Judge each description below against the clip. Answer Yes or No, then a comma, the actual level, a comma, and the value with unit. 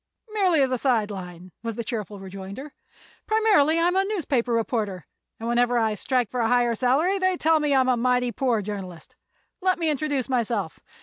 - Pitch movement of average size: No, wide, 5.8 semitones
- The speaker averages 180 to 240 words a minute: Yes, average, 185 wpm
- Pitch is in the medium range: No, high, 245 Hz